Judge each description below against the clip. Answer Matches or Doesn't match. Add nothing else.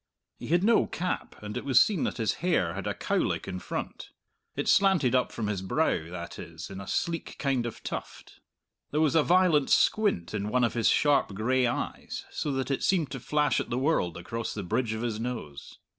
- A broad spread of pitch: Matches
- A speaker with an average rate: Doesn't match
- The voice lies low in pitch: Matches